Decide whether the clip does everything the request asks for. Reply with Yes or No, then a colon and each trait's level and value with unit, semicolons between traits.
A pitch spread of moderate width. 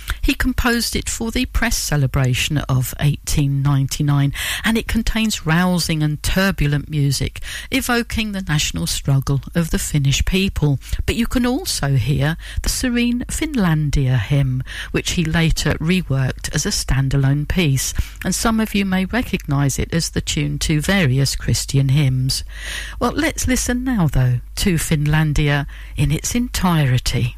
No: wide, 6.3 semitones